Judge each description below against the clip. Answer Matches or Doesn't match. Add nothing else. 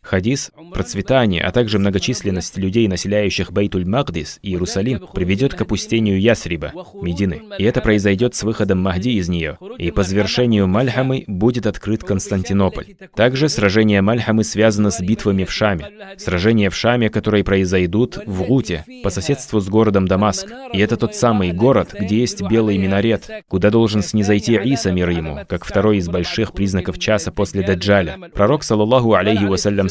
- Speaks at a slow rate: Doesn't match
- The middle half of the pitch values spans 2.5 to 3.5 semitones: Matches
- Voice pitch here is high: Doesn't match